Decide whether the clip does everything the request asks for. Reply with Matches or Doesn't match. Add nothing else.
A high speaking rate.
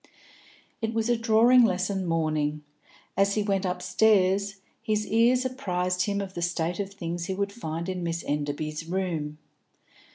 Doesn't match